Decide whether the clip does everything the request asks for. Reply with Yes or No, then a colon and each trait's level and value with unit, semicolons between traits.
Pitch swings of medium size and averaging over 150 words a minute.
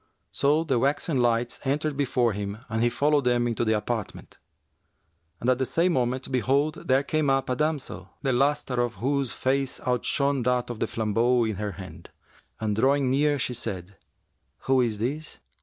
Yes: average, 3.3 semitones; average, 175 wpm